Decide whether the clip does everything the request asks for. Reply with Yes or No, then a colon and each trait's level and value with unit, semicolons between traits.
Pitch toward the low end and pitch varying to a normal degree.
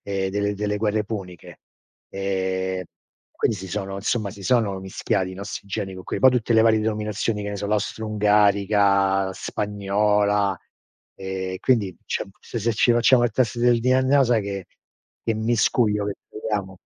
No: low, 105 Hz; narrow, 2.2 semitones